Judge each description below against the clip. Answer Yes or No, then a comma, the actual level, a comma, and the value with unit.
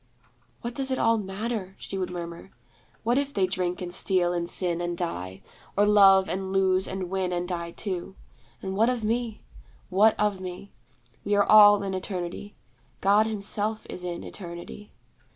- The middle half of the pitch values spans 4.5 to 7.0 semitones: No, average, 2.7 semitones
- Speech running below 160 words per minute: No, average, 170 wpm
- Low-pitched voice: No, high, 190 Hz